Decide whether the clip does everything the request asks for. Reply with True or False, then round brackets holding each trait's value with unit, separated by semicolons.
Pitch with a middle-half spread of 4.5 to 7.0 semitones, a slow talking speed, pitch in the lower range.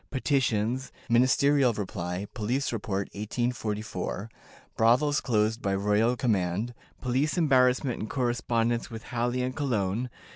False (3.2 semitones; 110 wpm; 120 Hz)